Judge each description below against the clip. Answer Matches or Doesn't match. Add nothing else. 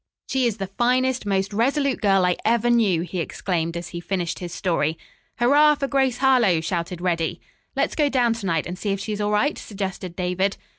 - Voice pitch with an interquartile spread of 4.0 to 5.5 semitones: Matches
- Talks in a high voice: Matches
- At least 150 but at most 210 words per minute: Matches